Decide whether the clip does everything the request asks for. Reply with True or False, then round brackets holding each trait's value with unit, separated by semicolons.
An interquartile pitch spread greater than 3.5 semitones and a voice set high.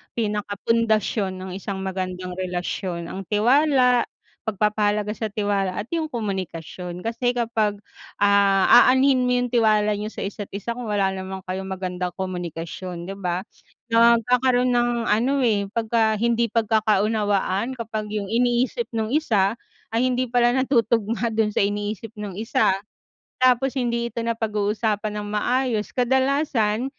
False (3.2 semitones; 215 Hz)